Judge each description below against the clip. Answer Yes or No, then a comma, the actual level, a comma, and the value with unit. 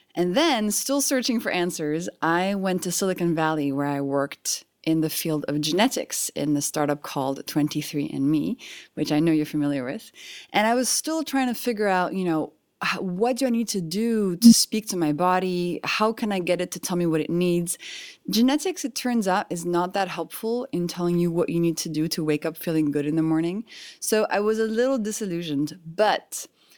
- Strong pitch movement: Yes, wide, 6.3 semitones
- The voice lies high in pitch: No, medium, 180 Hz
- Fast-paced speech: Yes, fast, 210 wpm